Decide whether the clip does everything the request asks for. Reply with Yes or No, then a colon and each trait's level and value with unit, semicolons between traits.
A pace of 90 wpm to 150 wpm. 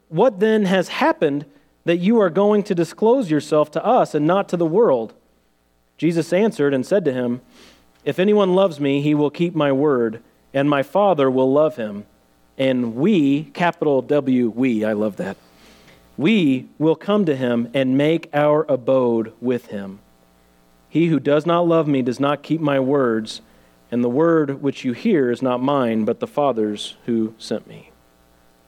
No: average, 175 wpm